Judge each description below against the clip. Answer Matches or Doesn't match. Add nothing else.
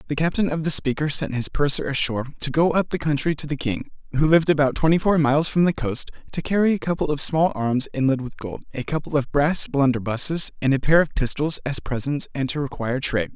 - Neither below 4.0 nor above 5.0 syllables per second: Doesn't match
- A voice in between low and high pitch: Matches